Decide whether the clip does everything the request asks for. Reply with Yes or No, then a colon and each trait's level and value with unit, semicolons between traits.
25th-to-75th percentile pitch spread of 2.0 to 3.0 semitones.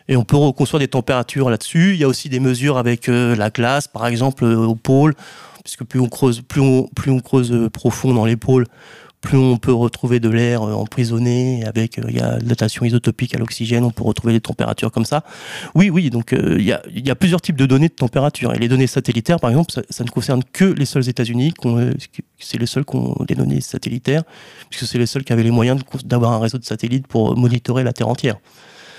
Yes: narrow, 2.4 semitones